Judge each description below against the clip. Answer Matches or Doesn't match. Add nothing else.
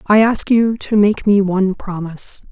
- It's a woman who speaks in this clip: Matches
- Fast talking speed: Doesn't match